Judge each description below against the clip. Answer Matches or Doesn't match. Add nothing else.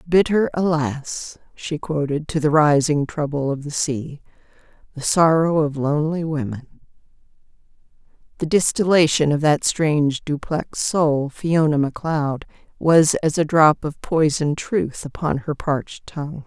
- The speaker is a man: Doesn't match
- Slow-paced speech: Matches